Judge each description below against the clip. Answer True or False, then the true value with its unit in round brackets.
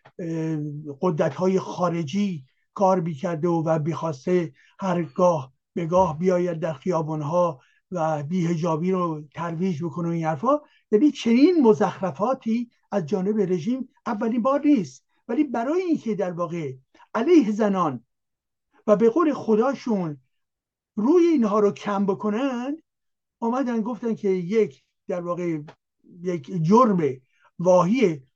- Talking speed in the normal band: True (125 wpm)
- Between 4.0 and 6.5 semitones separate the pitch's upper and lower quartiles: True (5.4 semitones)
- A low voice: False (185 Hz)